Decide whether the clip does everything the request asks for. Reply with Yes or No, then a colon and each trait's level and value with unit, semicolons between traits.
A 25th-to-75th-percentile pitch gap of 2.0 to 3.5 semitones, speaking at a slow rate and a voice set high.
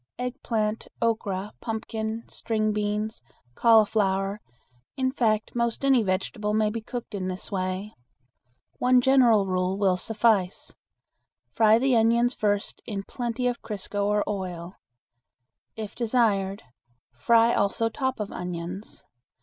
Yes: average, 2.8 semitones; slow, 120 wpm; high, 215 Hz